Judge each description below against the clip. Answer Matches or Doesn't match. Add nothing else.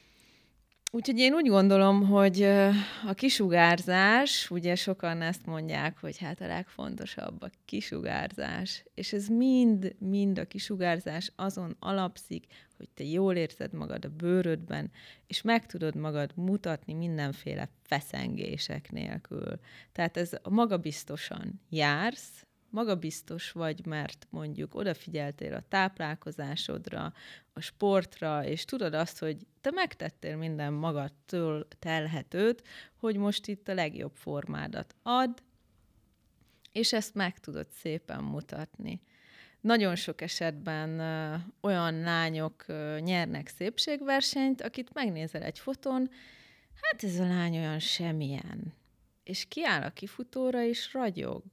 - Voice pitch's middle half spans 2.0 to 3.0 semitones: Doesn't match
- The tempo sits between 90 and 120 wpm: Matches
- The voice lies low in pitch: Doesn't match